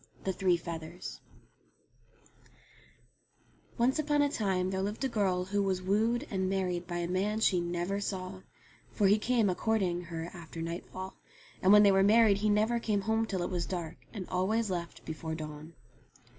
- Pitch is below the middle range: No, high, 190 Hz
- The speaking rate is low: No, average, 175 wpm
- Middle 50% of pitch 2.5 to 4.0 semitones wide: Yes, average, 3.3 semitones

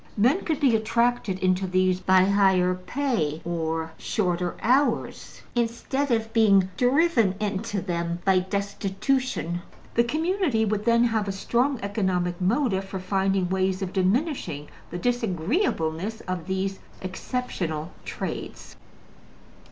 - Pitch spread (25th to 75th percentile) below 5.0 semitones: Yes, average, 4.4 semitones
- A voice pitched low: No, high, 195 Hz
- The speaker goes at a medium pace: No, slow, 120 wpm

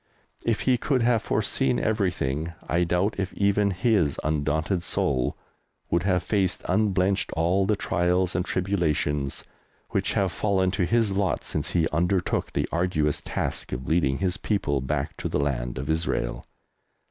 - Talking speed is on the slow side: No, average, 155 wpm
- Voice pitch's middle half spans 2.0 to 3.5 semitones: No, average, 4.3 semitones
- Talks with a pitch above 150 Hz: No, very low, 90 Hz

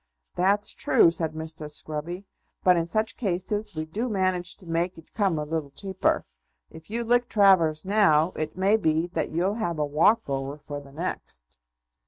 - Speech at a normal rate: Yes, average, 180 wpm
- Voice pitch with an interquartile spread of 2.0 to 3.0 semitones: No, average, 4.2 semitones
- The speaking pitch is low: No, medium, 170 Hz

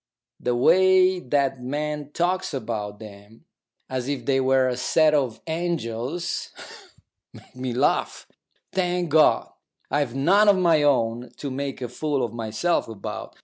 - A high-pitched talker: No, low, 135 Hz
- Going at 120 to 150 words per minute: Yes, average, 145 wpm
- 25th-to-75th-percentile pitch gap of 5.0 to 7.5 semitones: Yes, average, 5.3 semitones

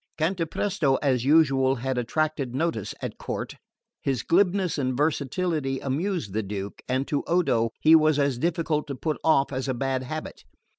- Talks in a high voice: No, medium, 140 Hz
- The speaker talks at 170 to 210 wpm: No, average, 160 wpm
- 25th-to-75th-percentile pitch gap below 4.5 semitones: Yes, average, 3.7 semitones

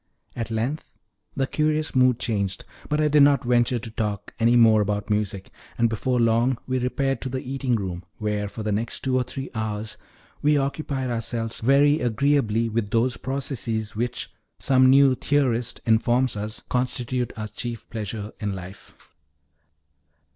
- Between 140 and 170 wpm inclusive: Yes, average, 160 wpm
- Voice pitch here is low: Yes, low, 120 Hz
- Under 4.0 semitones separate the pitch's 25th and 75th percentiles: Yes, average, 3.3 semitones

